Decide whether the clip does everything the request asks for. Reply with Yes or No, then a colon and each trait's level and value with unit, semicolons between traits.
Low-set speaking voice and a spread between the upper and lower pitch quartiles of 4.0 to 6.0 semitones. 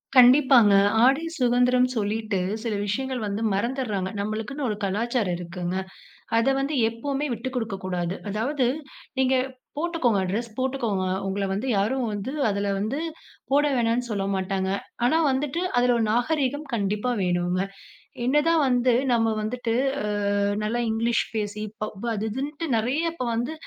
No: high, 235 Hz; average, 4.3 semitones